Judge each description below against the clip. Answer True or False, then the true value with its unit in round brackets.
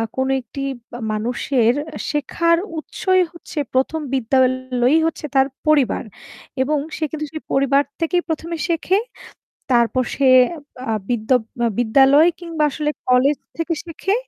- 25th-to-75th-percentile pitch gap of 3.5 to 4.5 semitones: True (4.0 semitones)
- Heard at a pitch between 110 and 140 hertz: False (280 Hz)